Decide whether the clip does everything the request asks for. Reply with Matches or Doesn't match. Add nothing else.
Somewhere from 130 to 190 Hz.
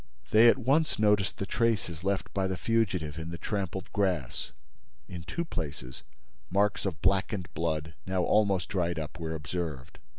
Doesn't match